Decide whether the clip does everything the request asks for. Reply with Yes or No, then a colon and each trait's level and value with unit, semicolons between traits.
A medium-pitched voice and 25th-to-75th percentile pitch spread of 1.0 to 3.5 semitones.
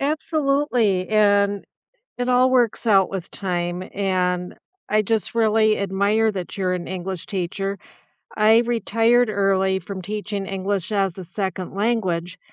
No: high, 200 Hz; average, 2.9 semitones